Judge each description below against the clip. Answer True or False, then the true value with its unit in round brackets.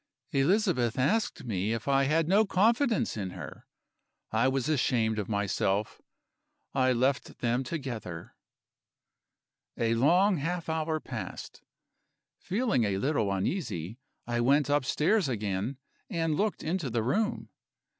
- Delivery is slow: True (125 wpm)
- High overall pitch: False (135 Hz)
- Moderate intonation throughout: False (6.8 semitones)